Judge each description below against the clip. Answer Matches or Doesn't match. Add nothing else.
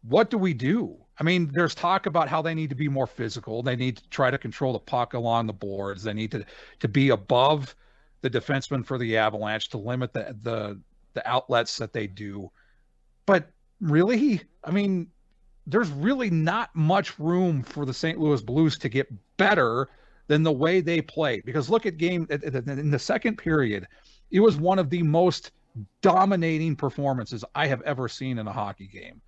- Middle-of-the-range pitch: Matches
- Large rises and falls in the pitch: Matches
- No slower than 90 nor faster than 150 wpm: Doesn't match